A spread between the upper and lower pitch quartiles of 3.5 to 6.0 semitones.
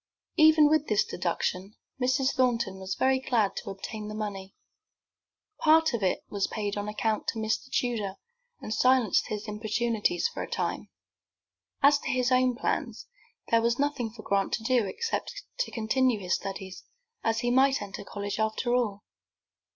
Yes: average, 4.0 semitones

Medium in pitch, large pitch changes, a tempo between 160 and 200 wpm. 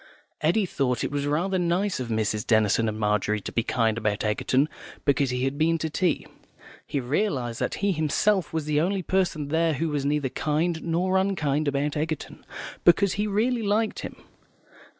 Yes: medium, 150 Hz; wide, 5.9 semitones; average, 180 wpm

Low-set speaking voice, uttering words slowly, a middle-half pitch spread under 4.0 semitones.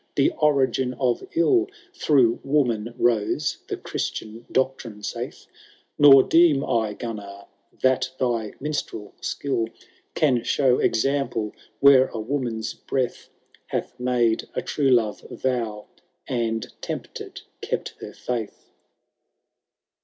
Yes: low, 125 Hz; slow, 115 wpm; average, 3.3 semitones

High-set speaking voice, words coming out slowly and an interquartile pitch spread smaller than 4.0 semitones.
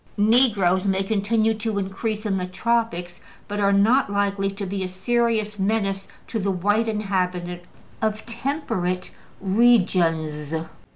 Yes: high, 200 Hz; slow, 130 wpm; average, 2.9 semitones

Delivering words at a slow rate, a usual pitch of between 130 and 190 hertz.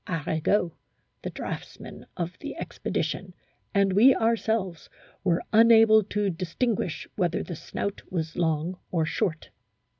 Yes: slow, 120 wpm; medium, 185 Hz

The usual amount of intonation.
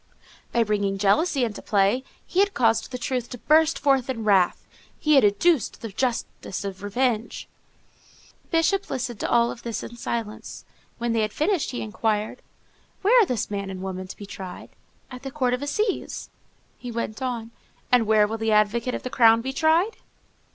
Yes: average, 4.0 semitones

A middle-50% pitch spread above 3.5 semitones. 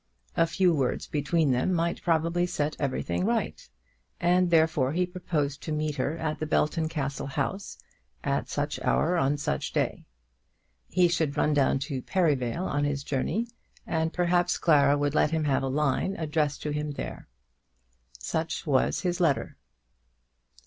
No: average, 3.2 semitones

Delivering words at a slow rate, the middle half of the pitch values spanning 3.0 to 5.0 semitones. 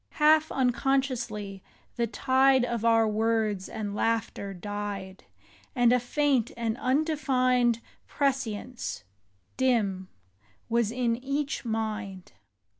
Yes: slow, 100 wpm; average, 3.7 semitones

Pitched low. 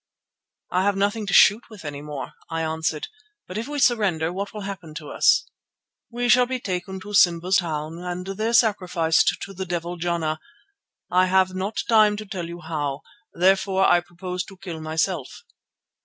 No: medium, 185 Hz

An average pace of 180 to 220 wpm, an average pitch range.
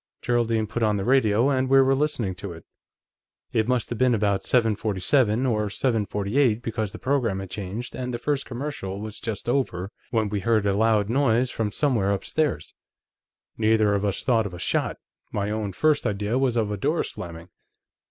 Yes: average, 185 wpm; average, 3.6 semitones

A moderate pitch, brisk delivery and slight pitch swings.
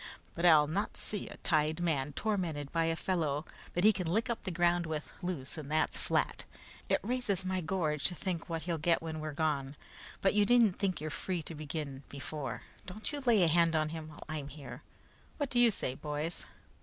No: medium, 165 Hz; fast, 210 wpm; average, 3.6 semitones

